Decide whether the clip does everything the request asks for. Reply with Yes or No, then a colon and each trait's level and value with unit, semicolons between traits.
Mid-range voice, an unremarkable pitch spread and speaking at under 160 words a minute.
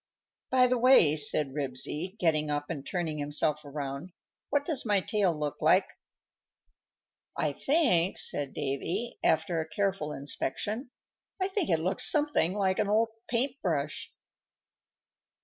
No: medium, 170 Hz; wide, 6.9 semitones; average, 140 wpm